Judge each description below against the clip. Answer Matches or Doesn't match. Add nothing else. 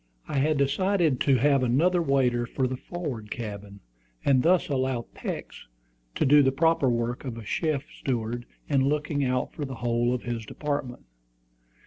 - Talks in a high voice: Doesn't match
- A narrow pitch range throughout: Doesn't match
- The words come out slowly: Doesn't match